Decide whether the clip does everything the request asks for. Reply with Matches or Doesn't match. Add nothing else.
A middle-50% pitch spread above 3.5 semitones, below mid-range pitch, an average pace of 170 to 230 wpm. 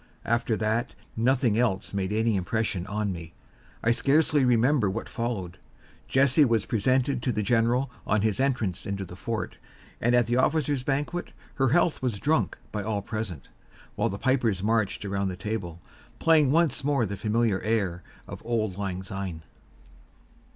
Doesn't match